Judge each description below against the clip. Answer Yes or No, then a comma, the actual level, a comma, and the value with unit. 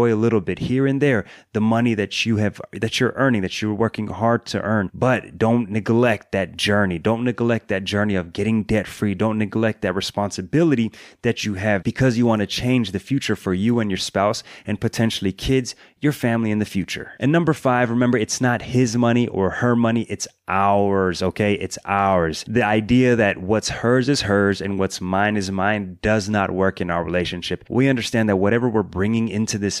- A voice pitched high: No, low, 110 Hz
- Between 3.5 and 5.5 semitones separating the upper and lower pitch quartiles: No, average, 3.1 semitones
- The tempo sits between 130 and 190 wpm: No, fast, 205 wpm